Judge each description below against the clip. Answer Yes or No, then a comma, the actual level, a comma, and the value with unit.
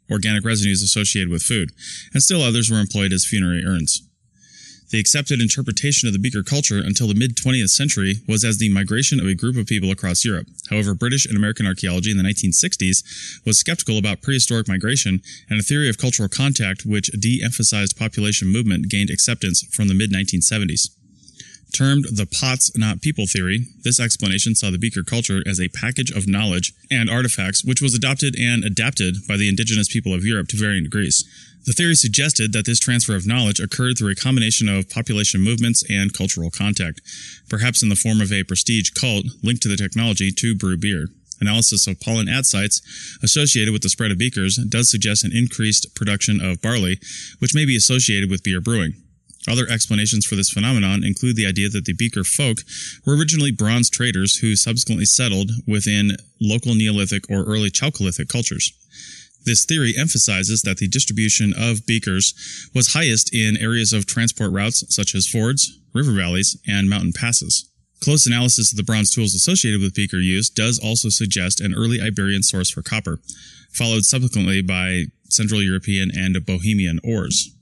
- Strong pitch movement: No, average, 3.2 semitones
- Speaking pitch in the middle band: No, low, 110 Hz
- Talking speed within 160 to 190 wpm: Yes, average, 180 wpm